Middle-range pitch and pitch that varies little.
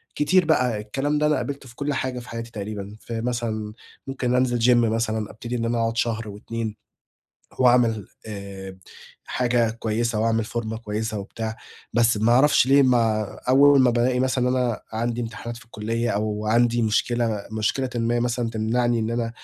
No: low, 115 Hz; narrow, 2.0 semitones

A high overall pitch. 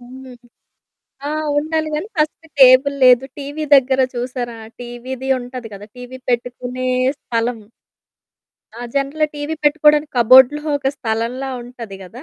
Yes: very high, 255 Hz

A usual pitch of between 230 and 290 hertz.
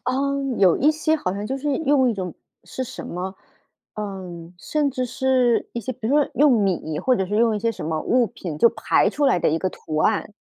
Yes: high, 235 Hz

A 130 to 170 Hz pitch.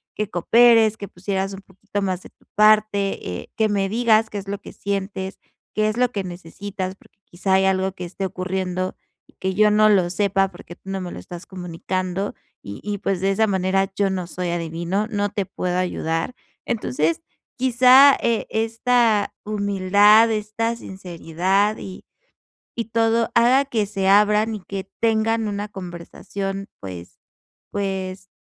No: high, 195 Hz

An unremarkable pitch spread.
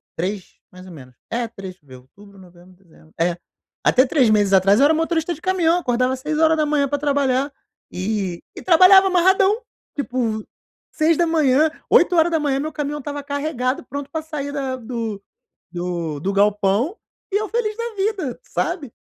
No: wide, 8.0 semitones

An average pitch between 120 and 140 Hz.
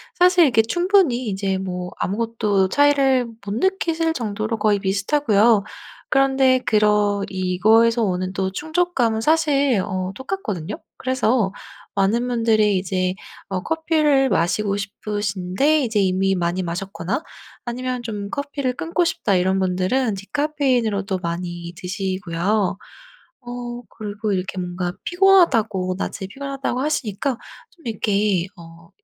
No: high, 215 Hz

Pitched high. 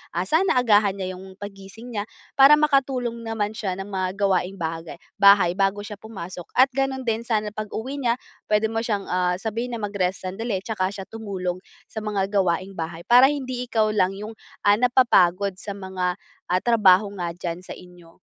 Yes: high, 205 Hz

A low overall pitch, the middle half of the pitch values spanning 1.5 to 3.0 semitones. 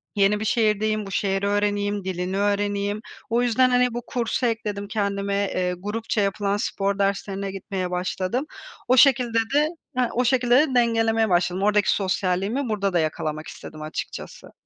No: high, 205 Hz; average, 2.7 semitones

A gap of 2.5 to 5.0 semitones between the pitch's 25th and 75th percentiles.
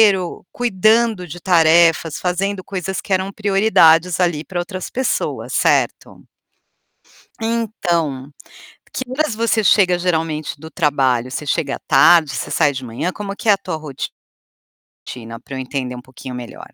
No: wide, 5.4 semitones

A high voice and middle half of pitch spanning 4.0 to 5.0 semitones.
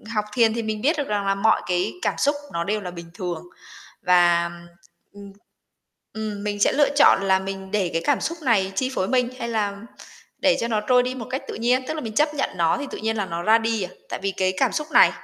Yes: high, 215 Hz; average, 4.6 semitones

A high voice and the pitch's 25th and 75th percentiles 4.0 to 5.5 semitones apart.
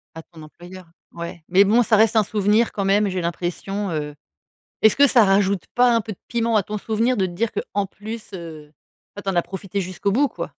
No: high, 200 Hz; average, 3.5 semitones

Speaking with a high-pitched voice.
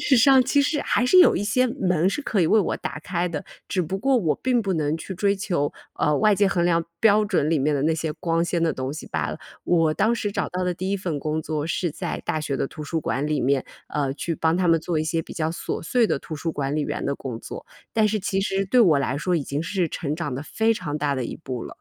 No: medium, 170 Hz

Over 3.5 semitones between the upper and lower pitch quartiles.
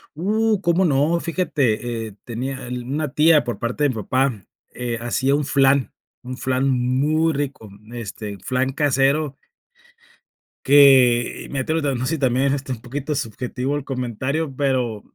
No: average, 2.9 semitones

